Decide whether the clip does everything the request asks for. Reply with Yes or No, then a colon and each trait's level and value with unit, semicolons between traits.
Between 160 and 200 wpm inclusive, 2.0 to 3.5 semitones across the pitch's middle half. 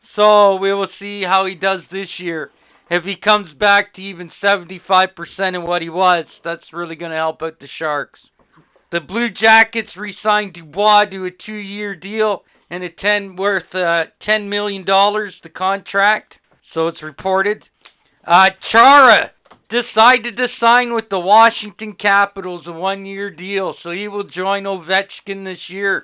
Yes: average, 165 wpm; narrow, 2.4 semitones